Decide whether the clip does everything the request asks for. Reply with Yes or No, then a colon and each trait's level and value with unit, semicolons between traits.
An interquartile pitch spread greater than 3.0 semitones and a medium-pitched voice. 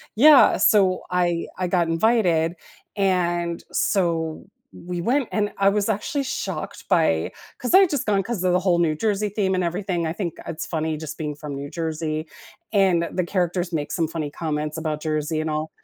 Yes: average, 3.7 semitones; medium, 175 Hz